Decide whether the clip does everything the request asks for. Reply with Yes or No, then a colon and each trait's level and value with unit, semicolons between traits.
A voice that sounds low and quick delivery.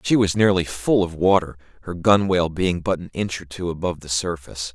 Yes: very low, 90 Hz; fast, 215 wpm